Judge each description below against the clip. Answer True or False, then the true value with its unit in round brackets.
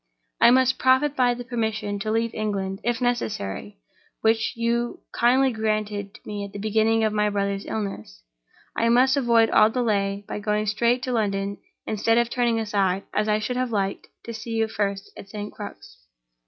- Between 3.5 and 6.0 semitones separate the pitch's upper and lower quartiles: False (2.7 semitones)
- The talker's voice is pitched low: False (220 Hz)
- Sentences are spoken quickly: False (185 wpm)